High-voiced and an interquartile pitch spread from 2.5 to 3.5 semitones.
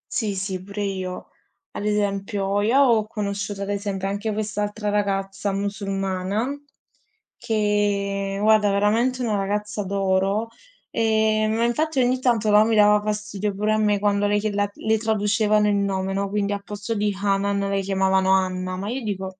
No: high, 205 Hz; narrow, 1.4 semitones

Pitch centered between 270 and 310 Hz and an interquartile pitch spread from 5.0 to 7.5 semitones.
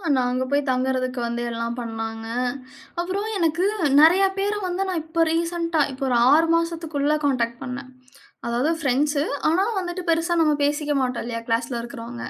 Yes: very high, 285 Hz; wide, 5.4 semitones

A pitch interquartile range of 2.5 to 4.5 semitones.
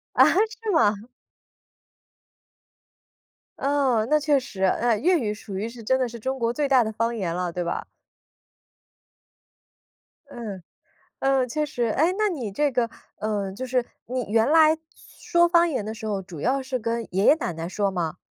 No: average, 5.3 semitones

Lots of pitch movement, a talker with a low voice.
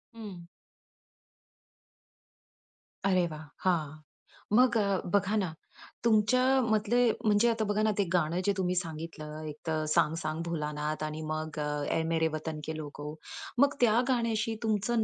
No: wide, 5.8 semitones; medium, 180 Hz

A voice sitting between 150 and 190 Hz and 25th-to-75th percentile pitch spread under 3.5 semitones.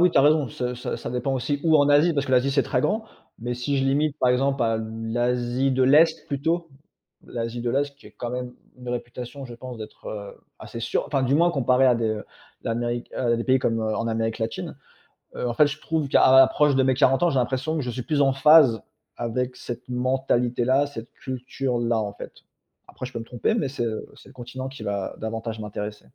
No: low, 125 Hz; average, 2.8 semitones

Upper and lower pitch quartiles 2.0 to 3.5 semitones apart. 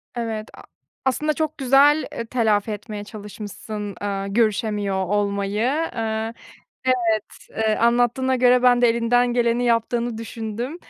Yes: average, 2.8 semitones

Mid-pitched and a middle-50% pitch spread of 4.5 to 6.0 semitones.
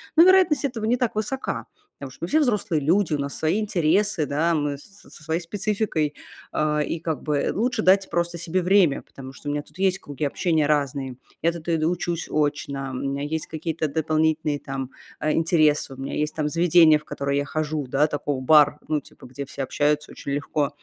No: medium, 155 Hz; average, 3.3 semitones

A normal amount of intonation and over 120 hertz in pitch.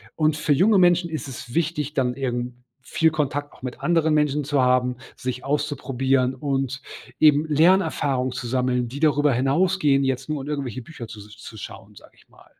Yes: average, 3.2 semitones; medium, 140 Hz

